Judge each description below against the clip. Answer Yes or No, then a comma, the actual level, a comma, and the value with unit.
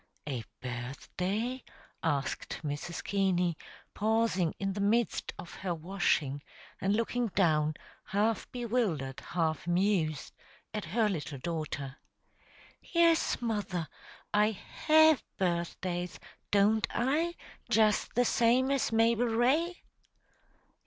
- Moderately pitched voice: No, high, 200 Hz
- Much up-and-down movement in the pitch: Yes, wide, 5.9 semitones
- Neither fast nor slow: No, slow, 105 wpm